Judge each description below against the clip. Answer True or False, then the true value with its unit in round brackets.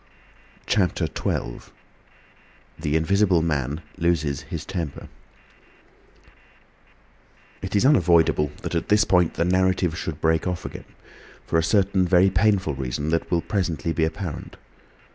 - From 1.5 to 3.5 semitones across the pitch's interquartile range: True (3.0 semitones)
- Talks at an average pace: False (125 wpm)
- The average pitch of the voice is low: True (85 Hz)